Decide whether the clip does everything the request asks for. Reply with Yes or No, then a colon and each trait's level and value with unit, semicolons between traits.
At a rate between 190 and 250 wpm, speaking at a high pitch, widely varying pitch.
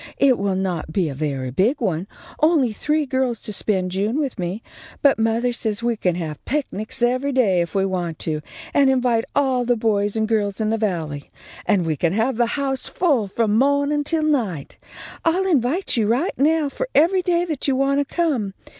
Yes: average, 200 wpm; high, 230 Hz; wide, 6.4 semitones